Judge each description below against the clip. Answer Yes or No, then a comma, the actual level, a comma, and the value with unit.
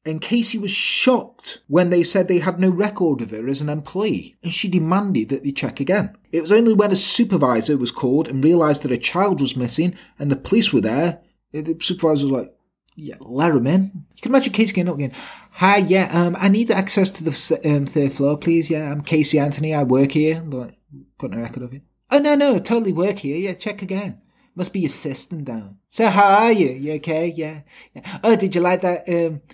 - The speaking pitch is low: No, medium, 170 Hz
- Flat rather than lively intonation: No, average, 5.0 semitones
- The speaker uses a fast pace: Yes, fast, 225 wpm